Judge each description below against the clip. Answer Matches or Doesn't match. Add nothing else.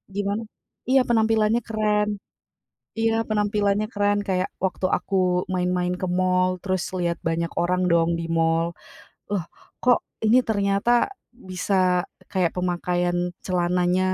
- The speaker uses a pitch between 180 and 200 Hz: Matches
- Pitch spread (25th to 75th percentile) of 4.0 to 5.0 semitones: Doesn't match